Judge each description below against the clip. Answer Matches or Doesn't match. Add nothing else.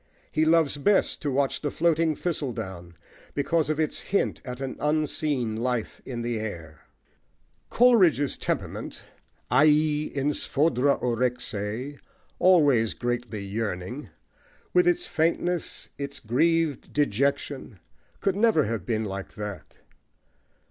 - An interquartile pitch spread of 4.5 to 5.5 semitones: Matches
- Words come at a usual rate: Doesn't match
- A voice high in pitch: Doesn't match